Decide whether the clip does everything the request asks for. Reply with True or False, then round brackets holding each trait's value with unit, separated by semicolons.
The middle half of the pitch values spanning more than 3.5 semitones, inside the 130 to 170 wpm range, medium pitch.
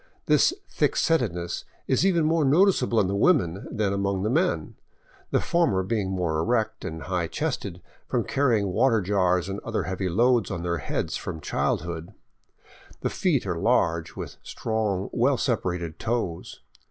False (5.6 semitones; 155 wpm; 100 Hz)